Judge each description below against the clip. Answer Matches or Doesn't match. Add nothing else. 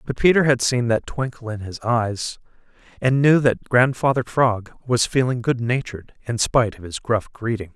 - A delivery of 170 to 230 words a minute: Matches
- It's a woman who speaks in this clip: Doesn't match